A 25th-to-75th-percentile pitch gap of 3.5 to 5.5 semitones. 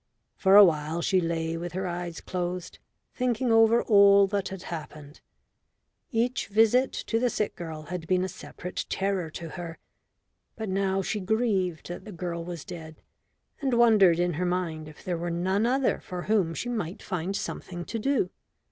Yes: average, 3.8 semitones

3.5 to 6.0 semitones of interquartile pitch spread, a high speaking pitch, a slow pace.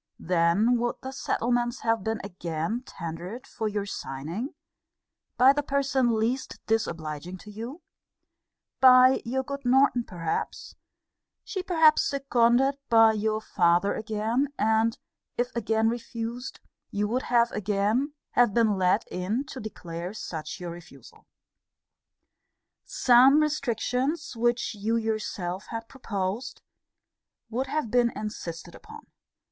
Yes: average, 4.1 semitones; high, 225 Hz; slow, 120 wpm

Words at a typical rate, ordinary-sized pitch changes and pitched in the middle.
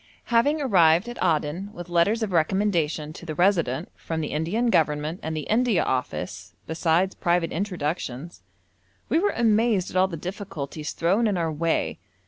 Yes: average, 160 wpm; average, 4.6 semitones; medium, 170 Hz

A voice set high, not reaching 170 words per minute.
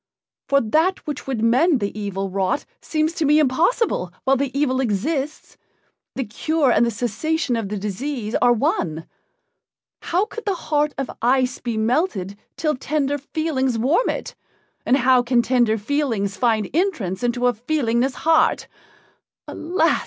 Yes: very high, 255 Hz; average, 150 wpm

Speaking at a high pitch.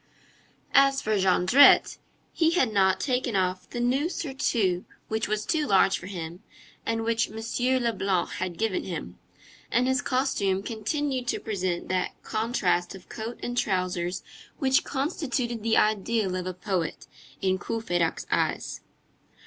Yes: high, 220 Hz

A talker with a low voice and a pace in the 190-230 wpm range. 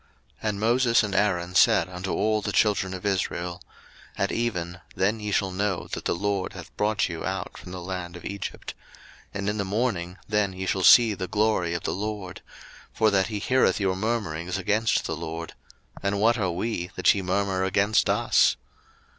Yes: low, 100 Hz; average, 195 wpm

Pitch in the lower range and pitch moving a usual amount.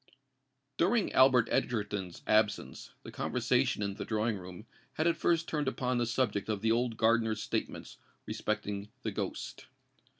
Yes: low, 115 Hz; average, 3.6 semitones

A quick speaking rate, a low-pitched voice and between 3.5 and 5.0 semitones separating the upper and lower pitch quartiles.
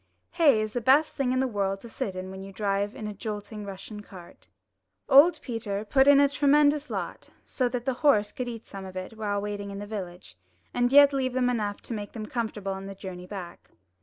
No: fast, 225 wpm; high, 215 Hz; average, 4.6 semitones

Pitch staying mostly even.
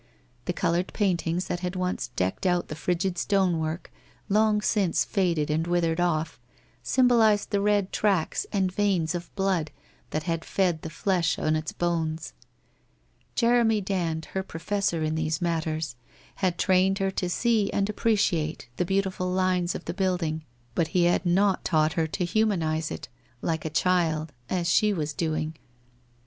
No: average, 3.3 semitones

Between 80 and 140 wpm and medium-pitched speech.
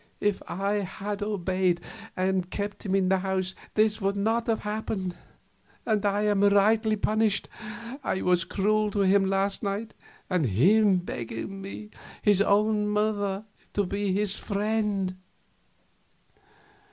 No: slow, 135 wpm; high, 200 Hz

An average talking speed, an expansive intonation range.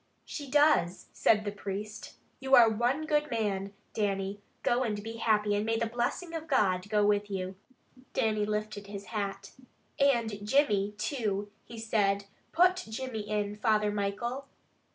No: average, 155 wpm; average, 2.8 semitones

